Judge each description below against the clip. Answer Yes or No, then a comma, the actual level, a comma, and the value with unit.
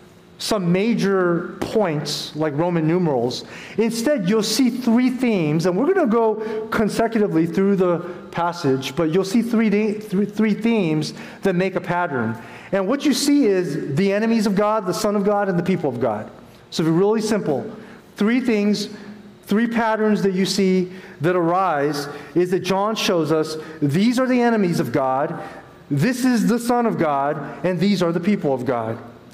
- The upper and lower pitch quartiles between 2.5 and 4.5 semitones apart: No, average, 4.9 semitones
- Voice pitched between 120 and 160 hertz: No, high, 190 Hz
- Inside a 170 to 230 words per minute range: Yes, average, 175 wpm